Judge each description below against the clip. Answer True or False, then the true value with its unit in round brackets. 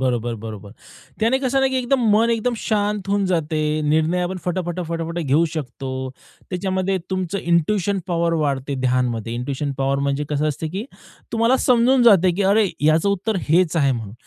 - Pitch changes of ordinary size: False (6.3 semitones)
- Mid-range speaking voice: True (170 Hz)